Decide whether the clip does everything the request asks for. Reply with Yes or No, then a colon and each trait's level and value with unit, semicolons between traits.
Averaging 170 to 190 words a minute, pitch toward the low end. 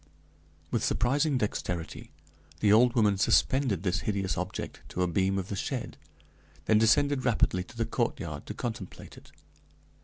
No: average, 150 wpm; low, 105 Hz